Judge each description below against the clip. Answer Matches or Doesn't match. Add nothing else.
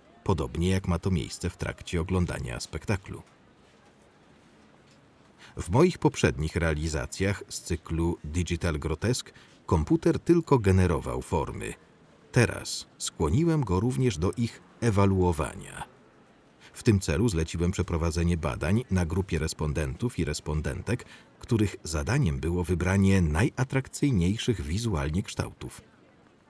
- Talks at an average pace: Doesn't match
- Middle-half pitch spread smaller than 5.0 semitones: Doesn't match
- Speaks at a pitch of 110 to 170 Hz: Doesn't match